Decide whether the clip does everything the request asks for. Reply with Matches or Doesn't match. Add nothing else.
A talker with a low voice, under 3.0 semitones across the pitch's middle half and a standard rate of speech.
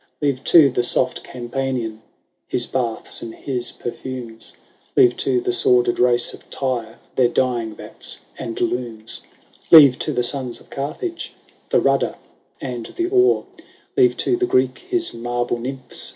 Matches